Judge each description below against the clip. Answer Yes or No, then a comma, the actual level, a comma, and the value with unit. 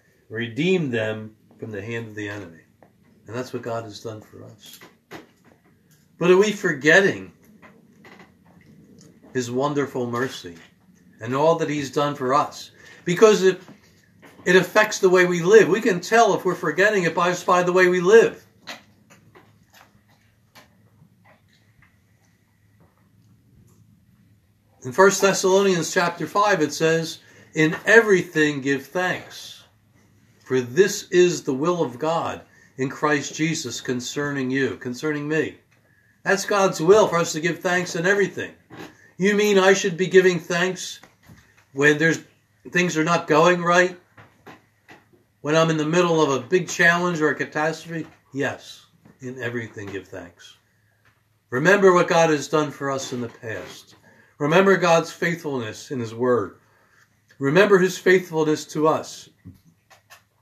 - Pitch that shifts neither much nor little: No, wide, 7.9 semitones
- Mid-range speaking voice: Yes, medium, 150 Hz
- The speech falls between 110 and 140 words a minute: Yes, slow, 135 wpm